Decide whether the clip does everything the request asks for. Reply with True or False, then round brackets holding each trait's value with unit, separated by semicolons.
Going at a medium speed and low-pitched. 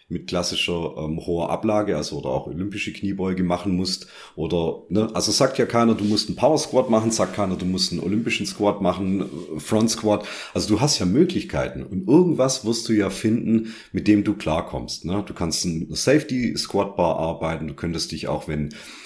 False (195 wpm; 95 Hz)